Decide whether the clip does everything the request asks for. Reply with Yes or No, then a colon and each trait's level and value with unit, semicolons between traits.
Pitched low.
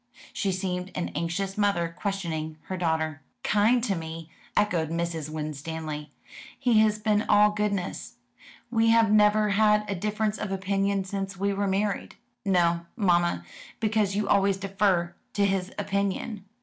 No: high, 195 Hz